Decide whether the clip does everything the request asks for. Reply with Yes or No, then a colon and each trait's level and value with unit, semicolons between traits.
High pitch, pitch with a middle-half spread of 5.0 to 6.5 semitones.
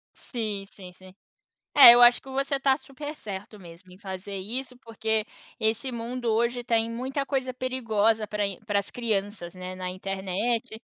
No: high, 220 Hz; average, 4.2 semitones